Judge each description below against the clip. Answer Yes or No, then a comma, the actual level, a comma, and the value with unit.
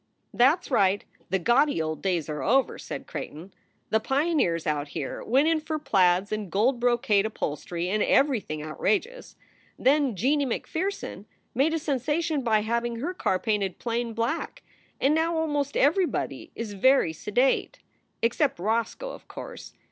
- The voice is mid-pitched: No, high, 235 Hz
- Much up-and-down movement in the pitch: Yes, wide, 7.1 semitones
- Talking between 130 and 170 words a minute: Yes, average, 155 wpm